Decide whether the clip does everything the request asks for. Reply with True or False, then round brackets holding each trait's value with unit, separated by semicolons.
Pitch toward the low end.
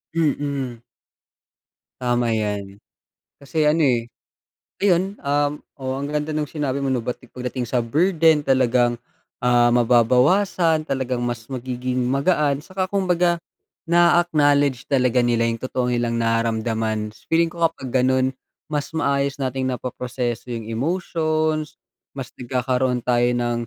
True (130 Hz)